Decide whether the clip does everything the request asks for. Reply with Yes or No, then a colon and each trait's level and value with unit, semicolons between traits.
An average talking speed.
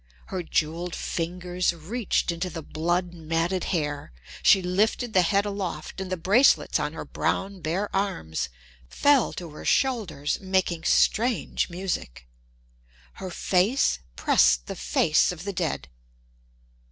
No: slow, 130 wpm